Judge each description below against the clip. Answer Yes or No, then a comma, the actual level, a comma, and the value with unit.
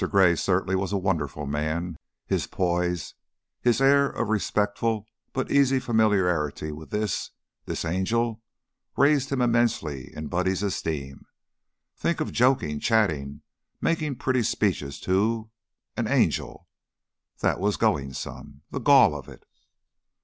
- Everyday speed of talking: No, slow, 130 wpm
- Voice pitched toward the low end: Yes, very low, 95 Hz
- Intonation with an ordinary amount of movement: No, wide, 6.9 semitones